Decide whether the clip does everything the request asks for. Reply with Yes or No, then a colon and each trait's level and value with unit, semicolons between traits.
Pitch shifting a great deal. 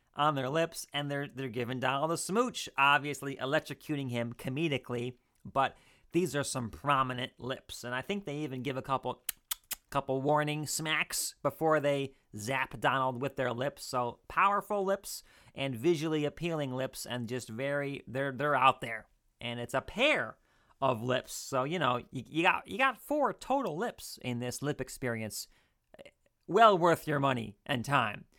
No: average, 3.3 semitones